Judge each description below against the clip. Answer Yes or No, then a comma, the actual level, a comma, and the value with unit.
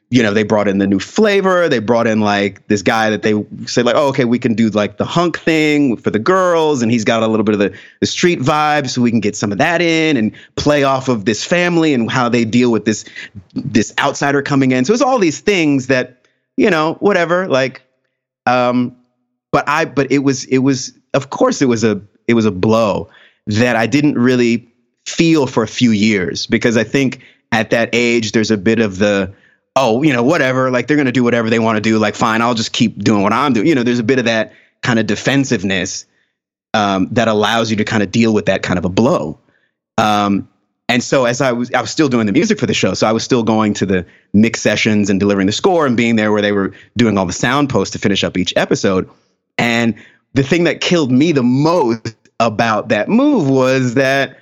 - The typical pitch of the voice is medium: No, low, 120 Hz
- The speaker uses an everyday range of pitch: Yes, average, 4.0 semitones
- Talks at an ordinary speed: No, fast, 235 wpm